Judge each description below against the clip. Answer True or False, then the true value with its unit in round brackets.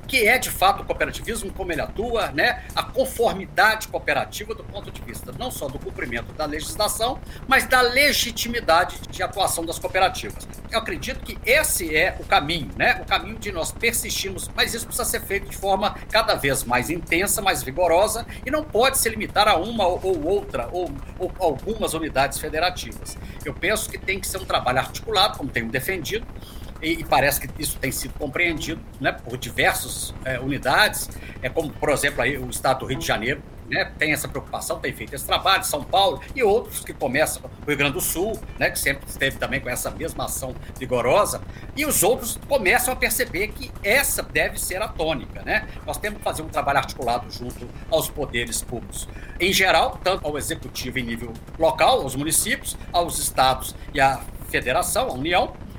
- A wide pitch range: True (6.0 semitones)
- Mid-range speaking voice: True (145 Hz)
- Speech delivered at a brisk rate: True (190 wpm)